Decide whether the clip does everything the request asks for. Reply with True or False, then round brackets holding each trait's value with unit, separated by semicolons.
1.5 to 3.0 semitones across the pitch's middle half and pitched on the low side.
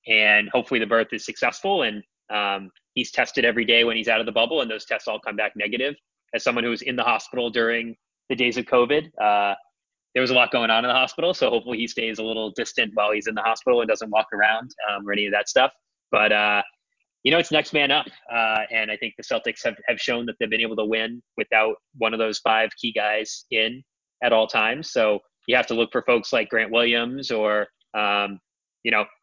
True (2.4 semitones; 110 Hz)